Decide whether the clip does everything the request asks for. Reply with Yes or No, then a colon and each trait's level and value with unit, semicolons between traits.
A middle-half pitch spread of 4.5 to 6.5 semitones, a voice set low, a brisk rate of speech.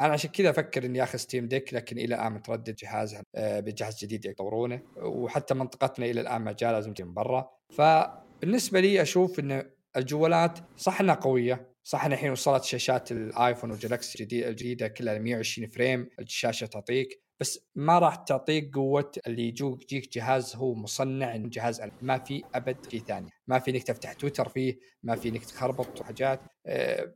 No: average, 3.1 semitones; low, 130 Hz; fast, 170 wpm